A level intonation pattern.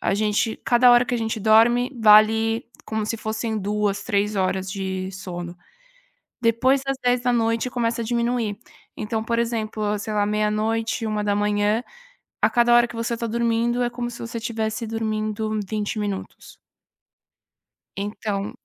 Yes: narrow, 2.0 semitones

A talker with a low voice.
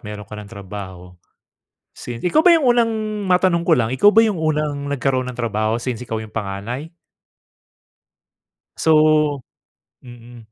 Yes: low, 125 Hz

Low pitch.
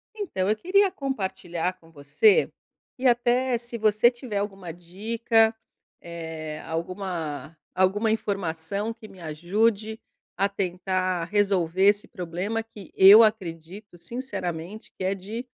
No: high, 195 Hz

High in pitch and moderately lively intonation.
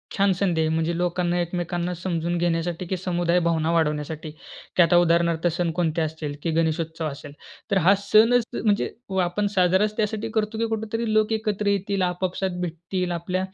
No: medium, 175 Hz; average, 3.2 semitones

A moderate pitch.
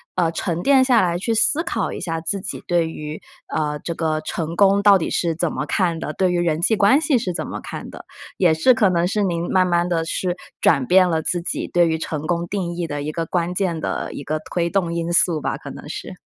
Yes: medium, 175 Hz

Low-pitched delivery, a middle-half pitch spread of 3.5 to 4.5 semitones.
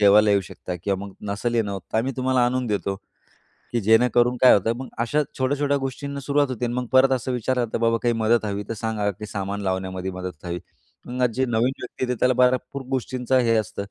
Yes: low, 120 Hz; average, 3.9 semitones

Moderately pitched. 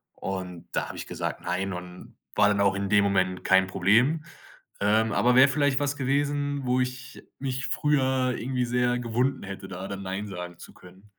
No: low, 110 Hz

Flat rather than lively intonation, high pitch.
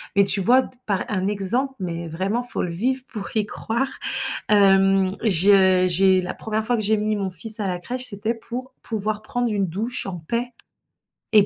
No: average, 3.4 semitones; high, 205 Hz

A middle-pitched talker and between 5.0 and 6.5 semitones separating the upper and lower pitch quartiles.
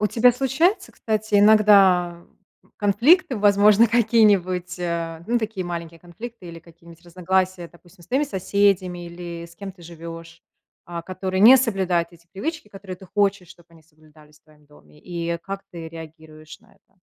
No: medium, 180 Hz; average, 3.5 semitones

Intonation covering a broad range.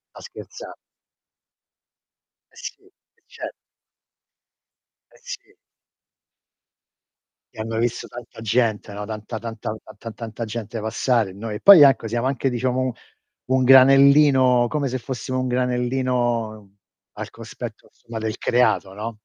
No: average, 2.7 semitones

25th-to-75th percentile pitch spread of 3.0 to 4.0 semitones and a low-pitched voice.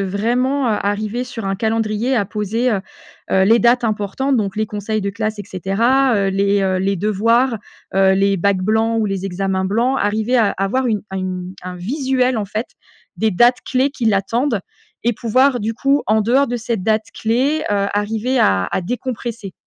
No: average, 3.6 semitones; high, 215 Hz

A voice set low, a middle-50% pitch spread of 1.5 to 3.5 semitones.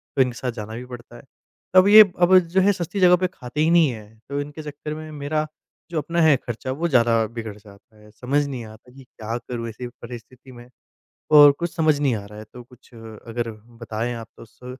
No: low, 125 Hz; average, 4.9 semitones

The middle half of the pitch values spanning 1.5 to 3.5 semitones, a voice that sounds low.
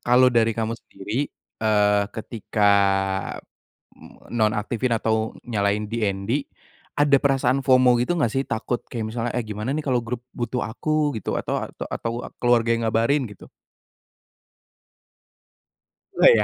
Yes: average, 2.8 semitones; low, 115 Hz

